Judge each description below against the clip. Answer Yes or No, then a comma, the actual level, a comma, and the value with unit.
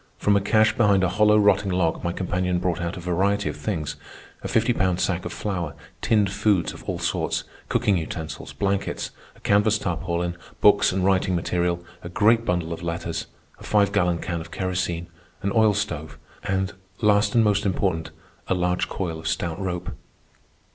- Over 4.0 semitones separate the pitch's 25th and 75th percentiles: No, average, 2.8 semitones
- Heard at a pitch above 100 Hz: No, very low, 90 Hz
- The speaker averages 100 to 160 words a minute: No, average, 175 wpm